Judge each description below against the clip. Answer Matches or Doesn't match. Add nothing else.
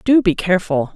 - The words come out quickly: Doesn't match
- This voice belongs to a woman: Matches